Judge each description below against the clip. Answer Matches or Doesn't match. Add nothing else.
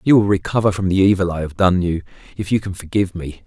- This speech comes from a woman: Doesn't match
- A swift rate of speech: Matches